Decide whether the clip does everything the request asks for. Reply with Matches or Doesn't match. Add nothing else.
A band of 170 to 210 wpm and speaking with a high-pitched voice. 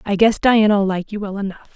Doesn't match